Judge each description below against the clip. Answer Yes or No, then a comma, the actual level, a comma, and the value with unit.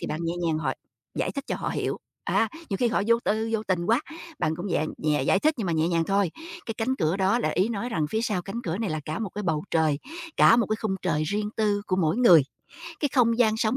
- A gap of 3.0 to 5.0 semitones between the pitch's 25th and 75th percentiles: No, wide, 5.4 semitones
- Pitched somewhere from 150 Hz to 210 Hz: Yes, high, 200 Hz